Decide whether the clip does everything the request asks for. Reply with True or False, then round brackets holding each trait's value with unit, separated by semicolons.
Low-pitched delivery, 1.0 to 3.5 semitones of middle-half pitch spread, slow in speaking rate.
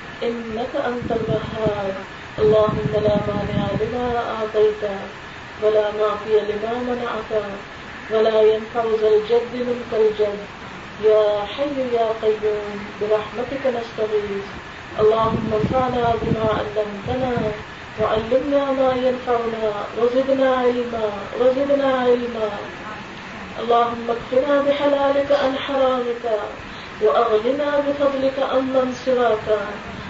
False (230 Hz; 3.0 semitones; 90 wpm)